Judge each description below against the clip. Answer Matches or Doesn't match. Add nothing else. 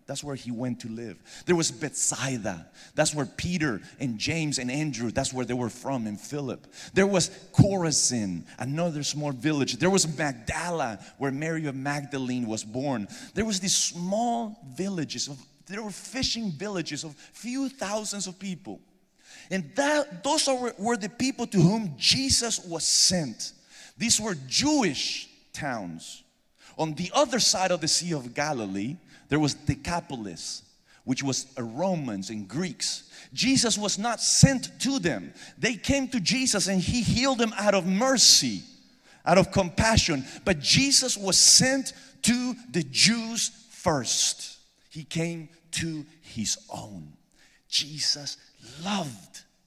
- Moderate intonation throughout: Doesn't match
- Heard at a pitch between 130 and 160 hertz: Doesn't match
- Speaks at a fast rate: Doesn't match